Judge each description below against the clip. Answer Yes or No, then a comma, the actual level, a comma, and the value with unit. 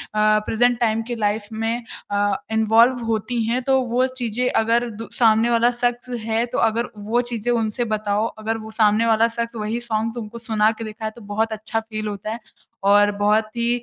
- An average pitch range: No, narrow, 1.7 semitones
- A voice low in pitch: No, high, 225 Hz